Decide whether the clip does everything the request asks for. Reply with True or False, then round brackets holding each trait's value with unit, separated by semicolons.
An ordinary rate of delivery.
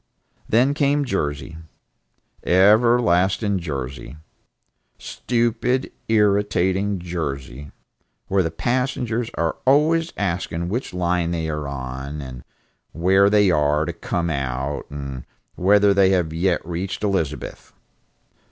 False (105 wpm)